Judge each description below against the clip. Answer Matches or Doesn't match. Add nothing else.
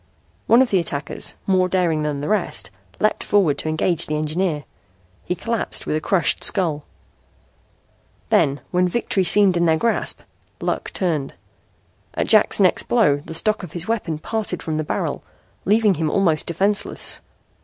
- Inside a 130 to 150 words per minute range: Doesn't match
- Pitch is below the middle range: Doesn't match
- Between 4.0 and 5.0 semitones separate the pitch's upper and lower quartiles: Matches